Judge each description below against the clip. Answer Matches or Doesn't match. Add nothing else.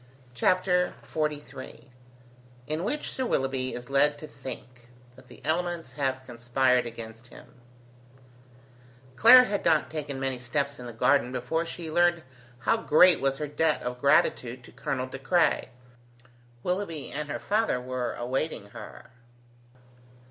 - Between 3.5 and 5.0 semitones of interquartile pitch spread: Matches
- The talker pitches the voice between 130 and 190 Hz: Matches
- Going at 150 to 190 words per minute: Doesn't match